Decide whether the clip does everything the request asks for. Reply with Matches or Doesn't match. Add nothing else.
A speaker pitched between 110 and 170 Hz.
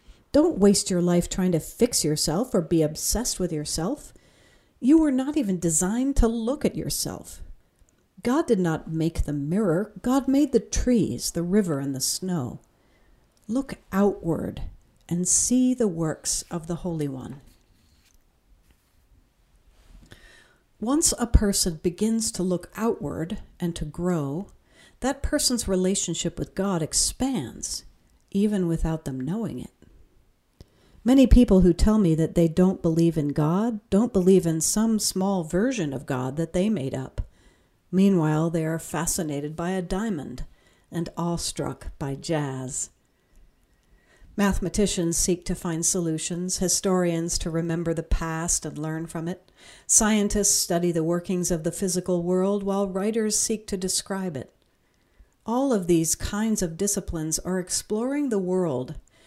Doesn't match